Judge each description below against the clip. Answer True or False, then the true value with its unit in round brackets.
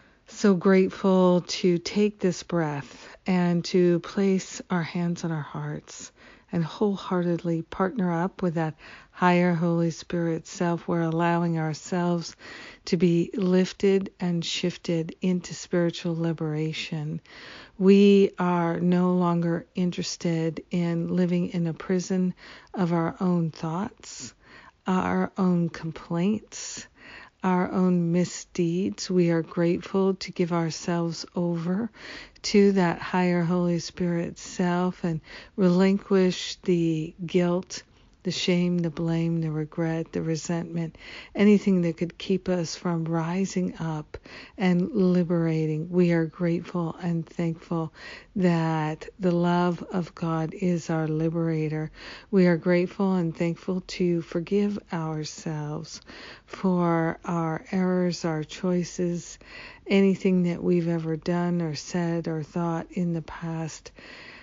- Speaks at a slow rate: True (120 wpm)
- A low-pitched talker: False (175 Hz)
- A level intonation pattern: True (1.8 semitones)